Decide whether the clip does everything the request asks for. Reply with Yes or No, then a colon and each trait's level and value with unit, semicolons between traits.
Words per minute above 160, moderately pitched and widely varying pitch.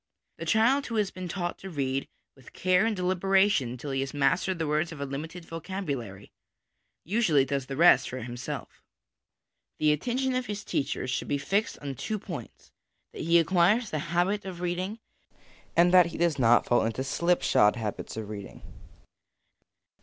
Yes: average, 170 wpm; medium, 170 Hz; wide, 5.8 semitones